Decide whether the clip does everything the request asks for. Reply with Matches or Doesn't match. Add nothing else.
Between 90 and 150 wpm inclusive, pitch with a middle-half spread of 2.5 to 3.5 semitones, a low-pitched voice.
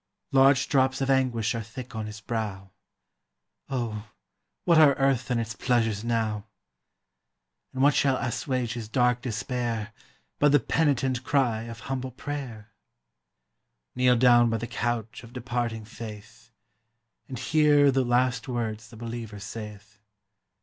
Matches